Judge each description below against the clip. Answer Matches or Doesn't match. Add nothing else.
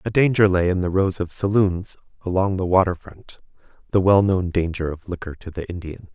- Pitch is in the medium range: Doesn't match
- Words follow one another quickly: Doesn't match